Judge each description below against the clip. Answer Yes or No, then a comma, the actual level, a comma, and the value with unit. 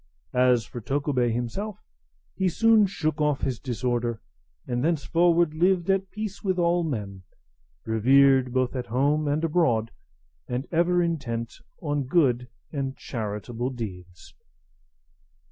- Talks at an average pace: No, slow, 125 wpm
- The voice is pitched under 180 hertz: Yes, medium, 140 Hz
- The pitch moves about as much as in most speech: No, wide, 5.8 semitones